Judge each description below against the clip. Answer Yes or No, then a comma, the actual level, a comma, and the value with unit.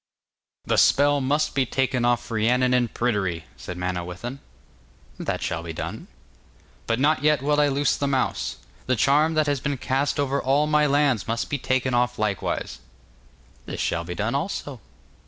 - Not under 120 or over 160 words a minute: No, average, 170 wpm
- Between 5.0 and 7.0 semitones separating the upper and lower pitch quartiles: No, average, 3.8 semitones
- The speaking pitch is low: Yes, low, 130 Hz